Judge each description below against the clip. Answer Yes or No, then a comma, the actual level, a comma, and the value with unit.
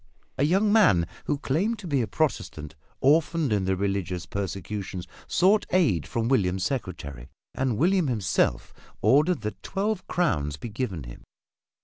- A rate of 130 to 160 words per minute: Yes, average, 145 wpm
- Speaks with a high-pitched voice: No, low, 115 Hz